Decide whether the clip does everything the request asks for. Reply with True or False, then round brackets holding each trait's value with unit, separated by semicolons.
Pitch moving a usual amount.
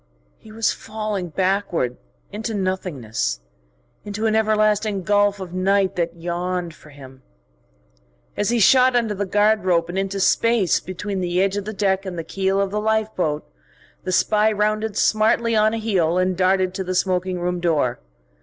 True (3.0 semitones)